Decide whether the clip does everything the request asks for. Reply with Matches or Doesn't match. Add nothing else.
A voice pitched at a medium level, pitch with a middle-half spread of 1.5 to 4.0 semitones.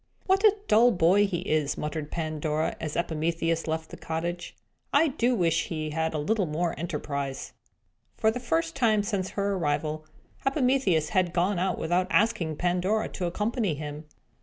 Doesn't match